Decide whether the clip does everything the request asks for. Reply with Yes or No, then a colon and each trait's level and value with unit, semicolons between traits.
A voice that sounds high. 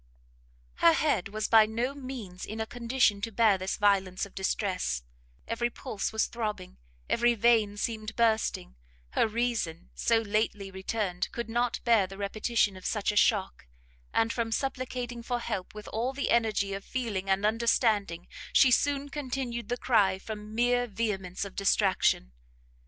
Yes: high, 220 Hz